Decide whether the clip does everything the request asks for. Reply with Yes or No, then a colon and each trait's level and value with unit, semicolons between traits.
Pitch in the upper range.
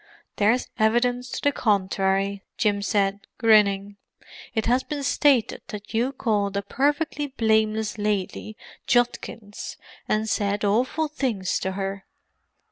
Yes: high, 215 Hz